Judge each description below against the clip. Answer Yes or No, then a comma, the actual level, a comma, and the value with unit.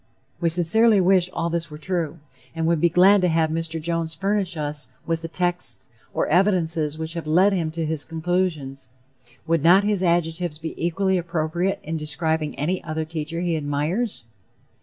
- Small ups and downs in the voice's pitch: Yes, narrow, 2.2 semitones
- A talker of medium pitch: Yes, medium, 165 Hz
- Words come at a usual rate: Yes, average, 175 wpm